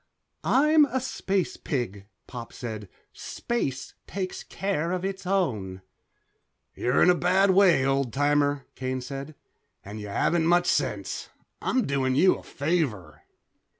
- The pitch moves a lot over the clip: Yes, wide, 6.6 semitones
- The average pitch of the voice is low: No, medium, 145 Hz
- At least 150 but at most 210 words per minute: No, slow, 135 wpm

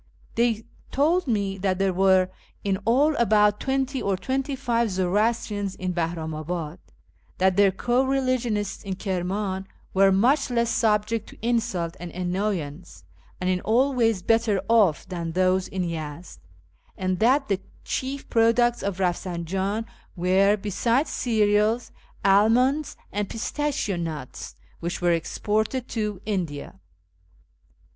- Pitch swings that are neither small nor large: Yes, average, 4.2 semitones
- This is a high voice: Yes, high, 205 Hz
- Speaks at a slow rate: Yes, slow, 125 wpm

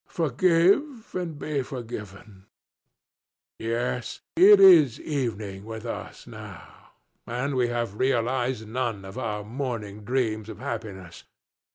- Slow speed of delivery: Yes, slow, 110 wpm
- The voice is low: Yes, low, 120 Hz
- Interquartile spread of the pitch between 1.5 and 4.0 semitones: No, average, 4.5 semitones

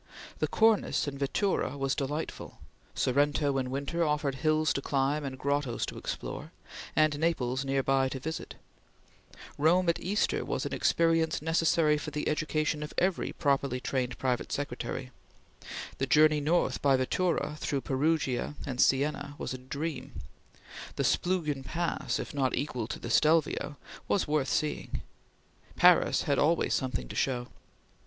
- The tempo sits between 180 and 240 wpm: No, average, 150 wpm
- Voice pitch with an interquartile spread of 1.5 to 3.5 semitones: Yes, average, 2.7 semitones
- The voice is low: No, medium, 145 Hz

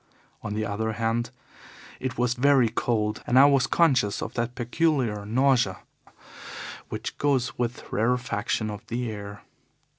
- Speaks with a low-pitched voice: Yes, low, 120 Hz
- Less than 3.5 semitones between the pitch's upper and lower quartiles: Yes, average, 3.0 semitones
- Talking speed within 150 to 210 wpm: No, average, 140 wpm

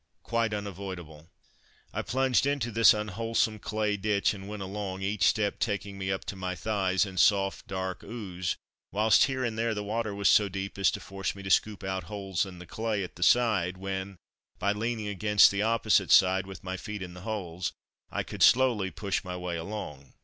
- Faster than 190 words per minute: Yes, average, 200 wpm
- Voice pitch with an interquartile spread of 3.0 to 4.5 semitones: No, narrow, 2.4 semitones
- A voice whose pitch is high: No, low, 100 Hz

